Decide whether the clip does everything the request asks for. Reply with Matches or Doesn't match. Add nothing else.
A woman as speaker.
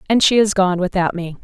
Matches